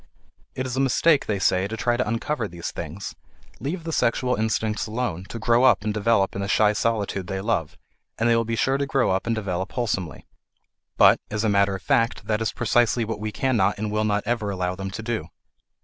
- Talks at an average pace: No, fast, 225 wpm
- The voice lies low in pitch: Yes, low, 110 Hz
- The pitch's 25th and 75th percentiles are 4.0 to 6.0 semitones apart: No, average, 3.2 semitones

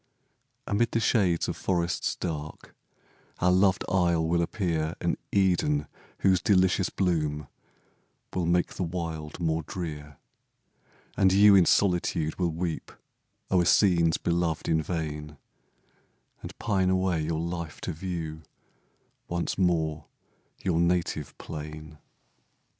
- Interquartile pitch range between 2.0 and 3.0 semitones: Yes, narrow, 2.6 semitones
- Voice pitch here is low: Yes, very low, 85 Hz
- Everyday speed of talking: No, slow, 120 wpm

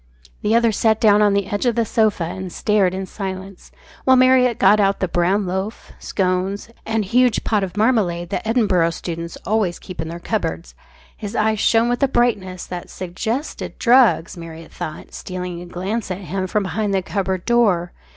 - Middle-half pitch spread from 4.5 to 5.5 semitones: No, average, 3.5 semitones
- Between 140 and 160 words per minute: No, average, 185 wpm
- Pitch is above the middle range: Yes, high, 195 Hz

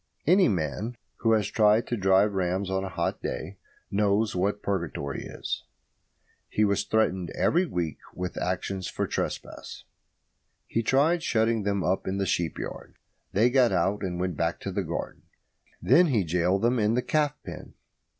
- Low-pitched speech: Yes, low, 100 Hz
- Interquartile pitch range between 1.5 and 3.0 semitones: No, average, 3.7 semitones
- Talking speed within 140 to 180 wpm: Yes, average, 170 wpm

